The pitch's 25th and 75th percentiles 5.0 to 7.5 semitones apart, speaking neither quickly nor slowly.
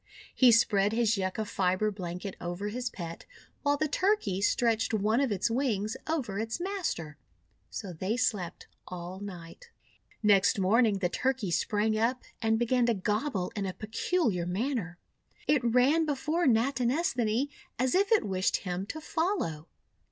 Yes: average, 5.3 semitones; average, 150 wpm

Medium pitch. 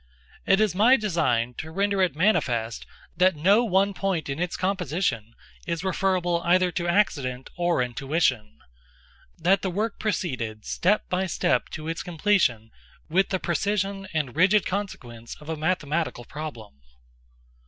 Yes: medium, 170 Hz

